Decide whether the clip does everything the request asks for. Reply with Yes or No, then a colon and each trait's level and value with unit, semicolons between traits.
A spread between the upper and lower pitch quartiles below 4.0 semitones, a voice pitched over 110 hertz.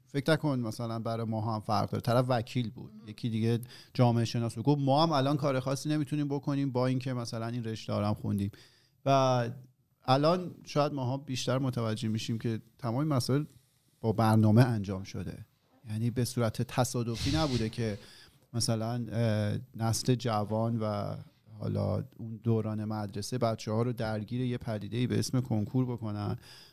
Yes: average, 2.9 semitones; low, 120 Hz